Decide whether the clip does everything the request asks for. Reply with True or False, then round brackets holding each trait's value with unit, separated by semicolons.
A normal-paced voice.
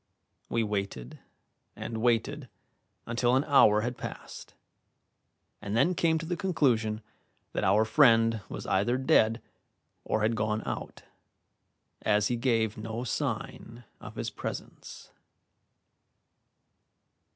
False (115 wpm)